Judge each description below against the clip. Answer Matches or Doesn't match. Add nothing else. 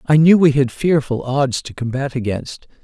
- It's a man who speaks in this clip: Matches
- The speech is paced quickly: Doesn't match